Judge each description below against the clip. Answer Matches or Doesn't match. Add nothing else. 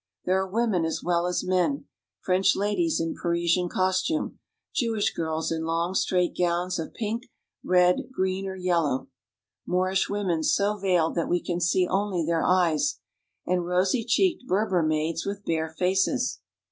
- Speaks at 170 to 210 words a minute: Doesn't match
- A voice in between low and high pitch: Matches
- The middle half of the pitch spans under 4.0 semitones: Matches